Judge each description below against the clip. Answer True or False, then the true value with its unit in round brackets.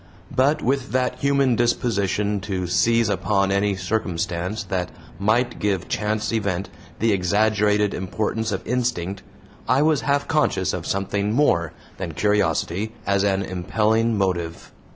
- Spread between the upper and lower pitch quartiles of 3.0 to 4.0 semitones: True (3.5 semitones)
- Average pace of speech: False (130 wpm)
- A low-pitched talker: True (105 Hz)